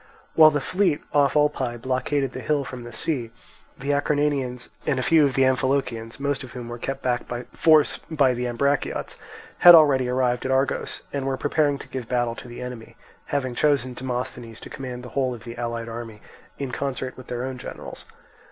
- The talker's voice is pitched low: Yes, low, 130 Hz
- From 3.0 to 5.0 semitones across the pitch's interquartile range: No, narrow, 2.5 semitones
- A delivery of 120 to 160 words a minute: No, average, 200 wpm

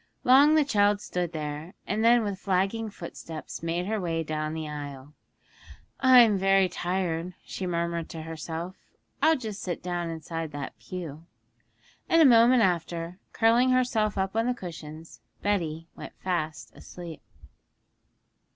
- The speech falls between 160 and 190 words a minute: No, average, 140 wpm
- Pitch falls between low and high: Yes, medium, 180 Hz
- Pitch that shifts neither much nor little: Yes, average, 4.8 semitones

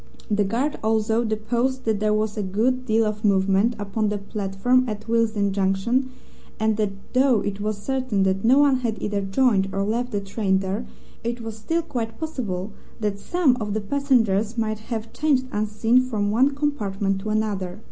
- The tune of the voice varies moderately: Yes, average, 3.4 semitones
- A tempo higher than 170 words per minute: Yes, average, 180 wpm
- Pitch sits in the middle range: No, high, 215 Hz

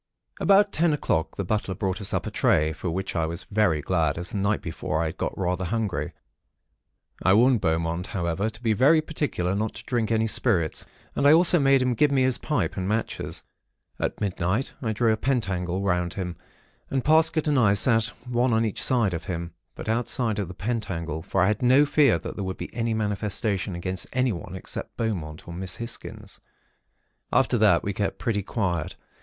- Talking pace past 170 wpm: Yes, average, 200 wpm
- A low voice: Yes, low, 105 Hz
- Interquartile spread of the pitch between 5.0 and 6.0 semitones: Yes, average, 5.3 semitones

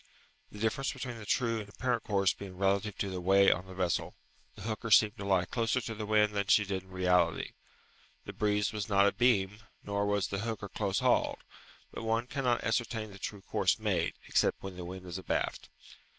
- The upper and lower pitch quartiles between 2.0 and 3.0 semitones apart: Yes, average, 2.7 semitones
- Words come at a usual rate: No, fast, 210 wpm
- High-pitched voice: No, low, 100 Hz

